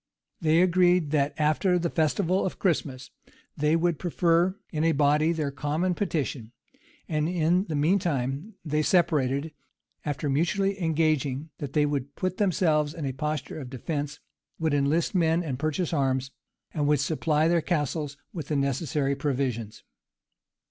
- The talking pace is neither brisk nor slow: Yes, average, 155 wpm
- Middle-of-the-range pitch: Yes, medium, 155 Hz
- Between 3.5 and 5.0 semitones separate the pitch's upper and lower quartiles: No, average, 3.1 semitones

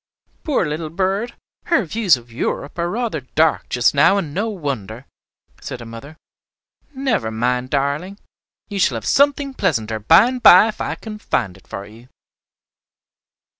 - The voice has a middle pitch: Yes, medium, 155 Hz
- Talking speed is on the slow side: No, average, 160 wpm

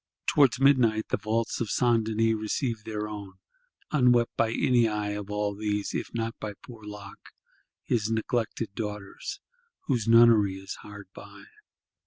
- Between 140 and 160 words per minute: Yes, average, 150 wpm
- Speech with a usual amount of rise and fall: No, narrow, 2.1 semitones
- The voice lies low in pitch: Yes, low, 110 Hz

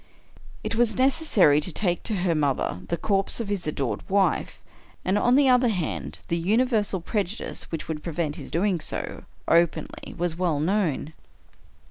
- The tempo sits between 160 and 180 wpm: Yes, average, 165 wpm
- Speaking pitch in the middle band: Yes, medium, 180 Hz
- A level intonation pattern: No, average, 5.1 semitones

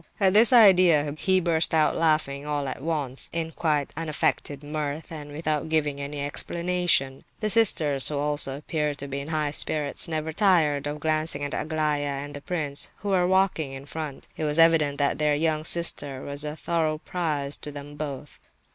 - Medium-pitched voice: Yes, medium, 150 Hz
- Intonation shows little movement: Yes, narrow, 2.3 semitones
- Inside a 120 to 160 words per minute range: No, average, 180 wpm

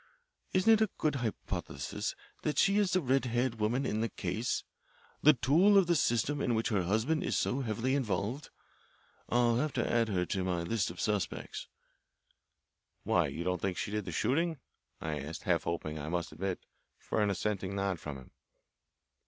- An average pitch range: No, wide, 6.8 semitones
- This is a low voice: Yes, low, 110 Hz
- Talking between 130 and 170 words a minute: No, average, 185 wpm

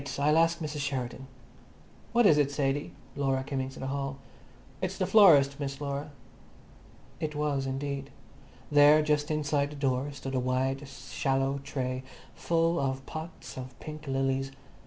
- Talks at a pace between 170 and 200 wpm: No, average, 150 wpm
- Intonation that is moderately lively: No, narrow, 1.9 semitones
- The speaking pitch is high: No, medium, 140 Hz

